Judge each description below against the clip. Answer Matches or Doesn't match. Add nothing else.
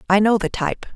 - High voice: Matches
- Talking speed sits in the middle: Doesn't match